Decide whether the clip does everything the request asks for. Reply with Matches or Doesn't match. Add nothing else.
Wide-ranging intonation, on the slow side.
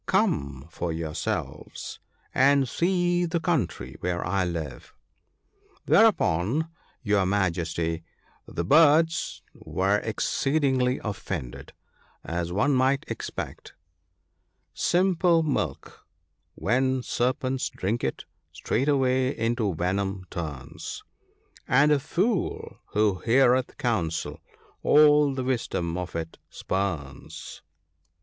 Matches